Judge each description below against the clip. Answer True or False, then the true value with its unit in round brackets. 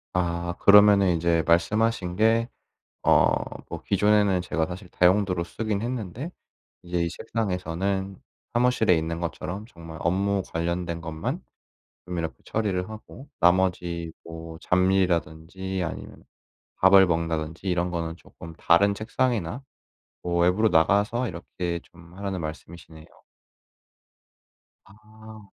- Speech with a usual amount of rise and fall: True (3.3 semitones)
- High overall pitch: False (90 Hz)